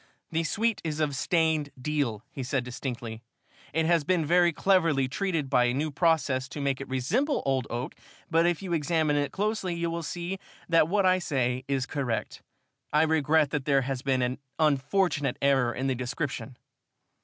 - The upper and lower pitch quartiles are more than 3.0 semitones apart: Yes, average, 4.1 semitones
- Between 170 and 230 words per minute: Yes, average, 180 wpm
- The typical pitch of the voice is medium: Yes, medium, 150 Hz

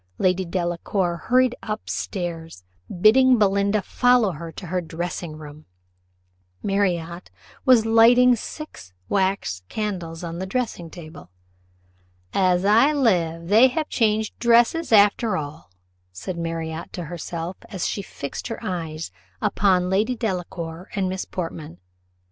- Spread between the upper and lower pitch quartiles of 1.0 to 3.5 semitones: No, average, 4.5 semitones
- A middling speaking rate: No, slow, 130 wpm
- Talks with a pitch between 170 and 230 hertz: Yes, medium, 185 Hz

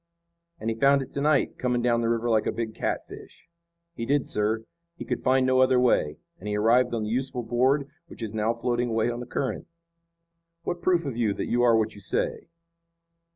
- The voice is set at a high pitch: No, low, 120 Hz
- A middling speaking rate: No, fast, 215 wpm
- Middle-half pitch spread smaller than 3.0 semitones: Yes, narrow, 2.5 semitones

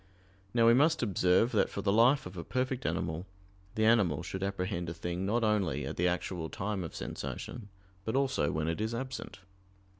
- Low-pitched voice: Yes, low, 100 Hz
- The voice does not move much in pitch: No, average, 4.9 semitones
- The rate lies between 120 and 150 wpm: No, average, 190 wpm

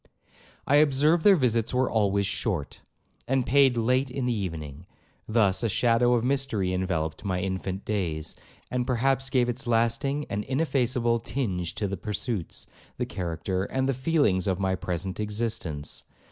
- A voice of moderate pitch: No, low, 115 Hz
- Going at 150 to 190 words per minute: Yes, average, 155 wpm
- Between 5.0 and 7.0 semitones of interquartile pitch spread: Yes, wide, 5.5 semitones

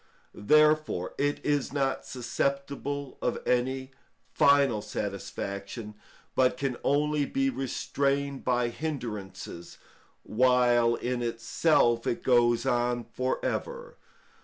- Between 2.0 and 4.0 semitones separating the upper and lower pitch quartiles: Yes, average, 3.0 semitones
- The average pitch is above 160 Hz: No, low, 130 Hz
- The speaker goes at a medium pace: No, slow, 100 wpm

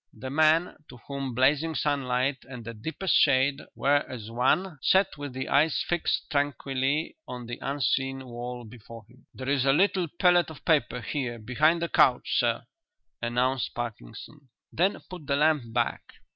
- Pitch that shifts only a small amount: No, average, 3.8 semitones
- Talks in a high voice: No, low, 135 Hz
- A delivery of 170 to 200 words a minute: No, average, 160 wpm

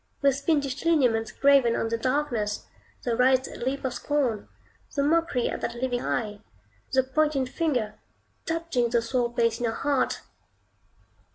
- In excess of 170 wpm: No, average, 150 wpm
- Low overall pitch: No, very high, 255 Hz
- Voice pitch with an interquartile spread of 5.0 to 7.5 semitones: No, average, 3.1 semitones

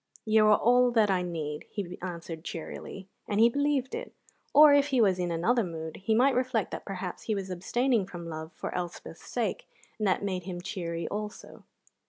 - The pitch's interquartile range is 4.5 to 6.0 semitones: Yes, wide, 5.4 semitones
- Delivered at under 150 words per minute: No, average, 190 wpm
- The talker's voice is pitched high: Yes, high, 195 Hz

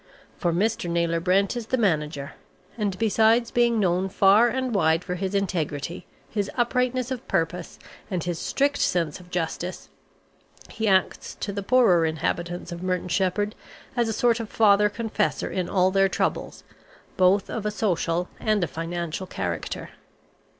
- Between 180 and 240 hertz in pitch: Yes, high, 190 Hz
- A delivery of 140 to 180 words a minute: Yes, average, 155 wpm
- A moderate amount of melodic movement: Yes, average, 4.2 semitones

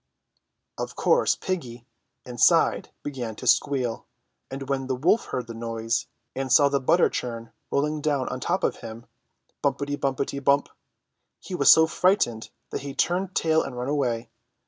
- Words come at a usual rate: Yes, average, 170 wpm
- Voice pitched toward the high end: No, low, 135 Hz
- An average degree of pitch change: Yes, average, 3.5 semitones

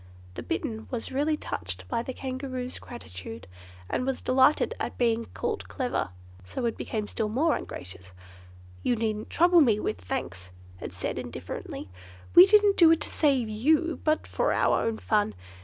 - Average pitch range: No, wide, 6.2 semitones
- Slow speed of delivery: No, average, 165 wpm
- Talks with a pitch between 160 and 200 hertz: No, high, 245 Hz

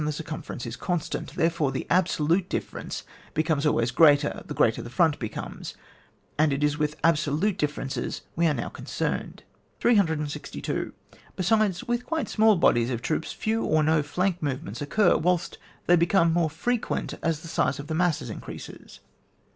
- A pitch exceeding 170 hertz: No, medium, 160 Hz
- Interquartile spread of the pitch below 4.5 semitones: Yes, average, 3.3 semitones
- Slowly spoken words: No, average, 170 wpm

